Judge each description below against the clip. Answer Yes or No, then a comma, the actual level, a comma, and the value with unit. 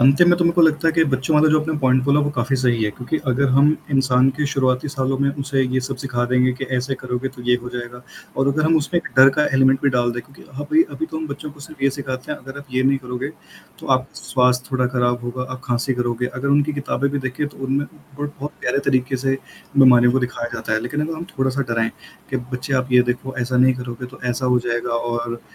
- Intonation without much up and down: Yes, narrow, 2.1 semitones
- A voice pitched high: No, low, 130 Hz